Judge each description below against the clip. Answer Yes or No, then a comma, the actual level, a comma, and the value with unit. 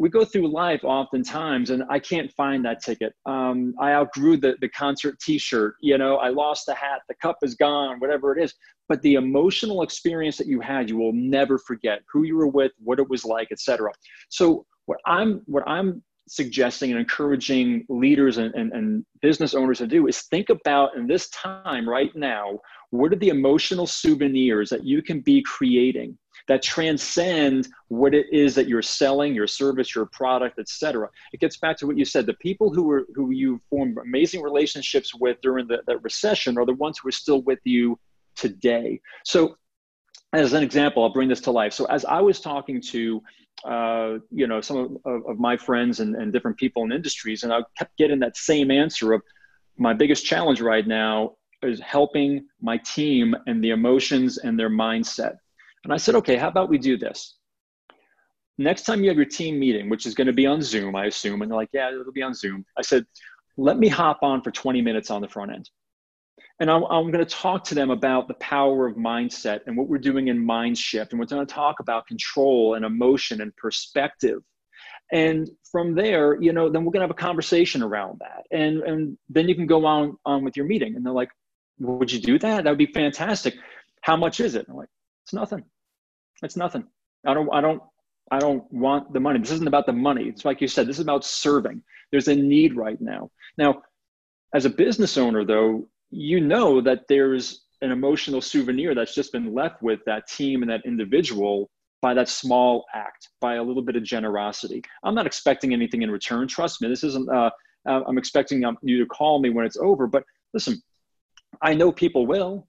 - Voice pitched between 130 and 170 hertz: Yes, medium, 140 Hz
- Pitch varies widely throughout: No, average, 4.4 semitones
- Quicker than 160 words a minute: Yes, fast, 205 wpm